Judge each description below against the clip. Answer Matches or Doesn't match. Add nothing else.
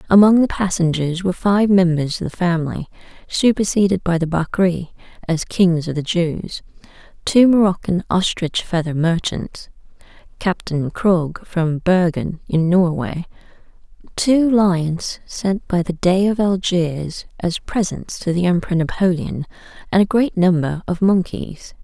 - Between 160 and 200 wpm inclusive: Doesn't match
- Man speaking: Doesn't match